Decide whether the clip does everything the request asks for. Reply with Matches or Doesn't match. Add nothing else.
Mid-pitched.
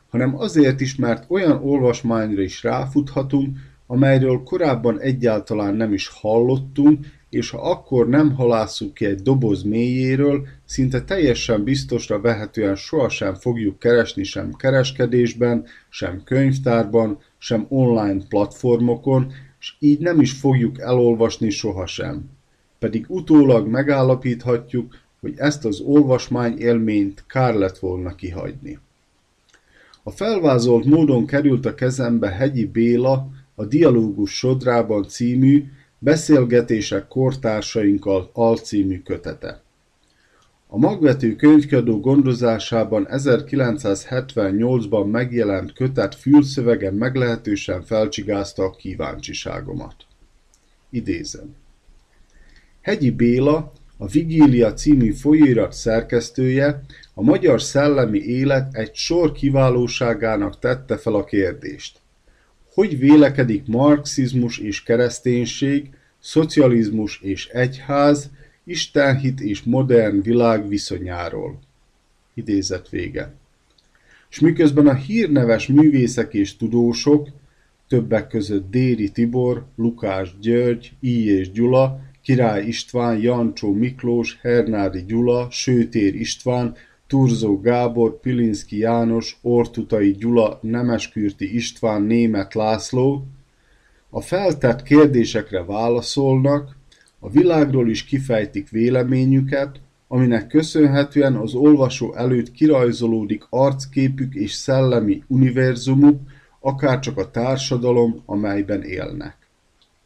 Doesn't match